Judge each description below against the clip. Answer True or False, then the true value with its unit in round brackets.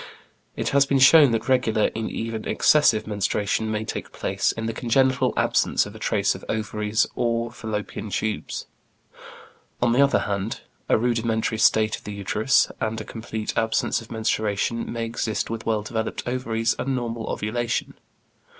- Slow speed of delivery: False (160 wpm)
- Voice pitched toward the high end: False (115 Hz)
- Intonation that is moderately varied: False (1.7 semitones)